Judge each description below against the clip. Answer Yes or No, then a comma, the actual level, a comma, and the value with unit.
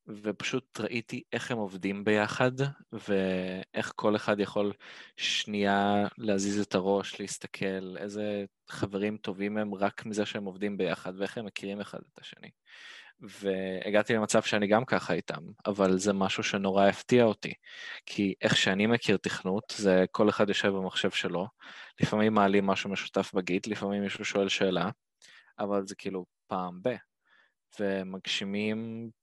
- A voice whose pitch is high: No, low, 100 Hz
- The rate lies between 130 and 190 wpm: Yes, average, 140 wpm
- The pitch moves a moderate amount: No, narrow, 1.7 semitones